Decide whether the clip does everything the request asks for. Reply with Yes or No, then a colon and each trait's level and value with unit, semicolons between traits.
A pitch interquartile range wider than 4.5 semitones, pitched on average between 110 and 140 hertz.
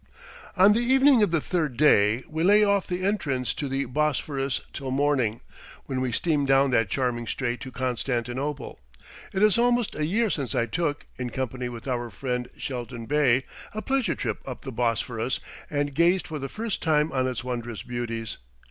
Yes: average, 5.3 semitones; low, 135 Hz